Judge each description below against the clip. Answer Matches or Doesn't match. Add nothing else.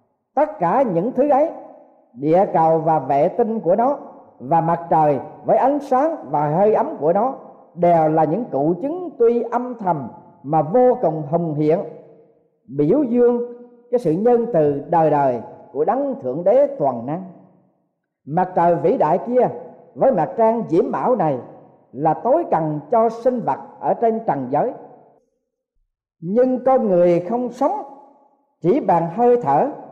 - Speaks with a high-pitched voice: Matches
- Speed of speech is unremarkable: Doesn't match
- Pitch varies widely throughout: Matches